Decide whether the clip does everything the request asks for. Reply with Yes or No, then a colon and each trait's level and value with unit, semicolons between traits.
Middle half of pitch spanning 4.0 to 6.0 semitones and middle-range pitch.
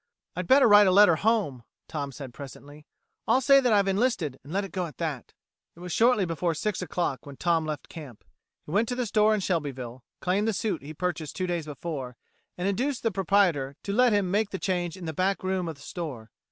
Yes: average, 5.2 semitones; medium, 180 Hz